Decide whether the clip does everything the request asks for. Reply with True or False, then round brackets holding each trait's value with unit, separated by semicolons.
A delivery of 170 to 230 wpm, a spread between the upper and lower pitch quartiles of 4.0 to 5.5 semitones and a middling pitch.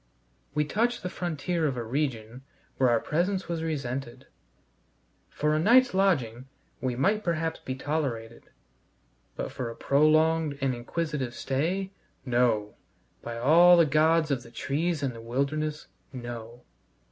False (140 wpm; 5.1 semitones; 145 Hz)